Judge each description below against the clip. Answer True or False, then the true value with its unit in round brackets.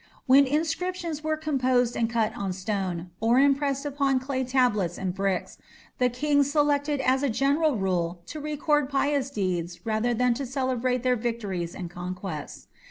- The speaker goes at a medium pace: True (160 wpm)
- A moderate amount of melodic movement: False (6.2 semitones)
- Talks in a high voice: True (255 Hz)